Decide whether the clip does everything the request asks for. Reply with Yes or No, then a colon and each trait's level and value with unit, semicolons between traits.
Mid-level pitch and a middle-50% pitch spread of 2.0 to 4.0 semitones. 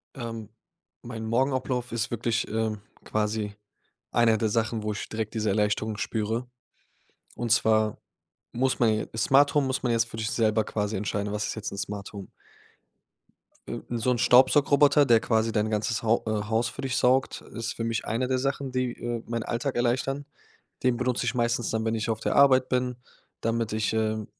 No: low, 115 Hz; narrow, 2.4 semitones